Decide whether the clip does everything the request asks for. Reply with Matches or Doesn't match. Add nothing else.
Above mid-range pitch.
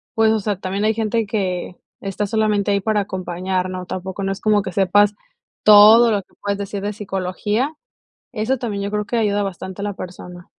Matches